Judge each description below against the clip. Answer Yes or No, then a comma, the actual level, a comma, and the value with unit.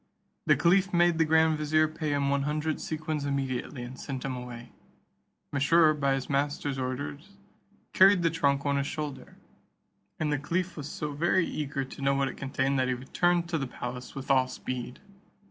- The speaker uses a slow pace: No, average, 185 wpm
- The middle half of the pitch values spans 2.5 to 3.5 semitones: Yes, average, 2.8 semitones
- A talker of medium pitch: Yes, medium, 145 Hz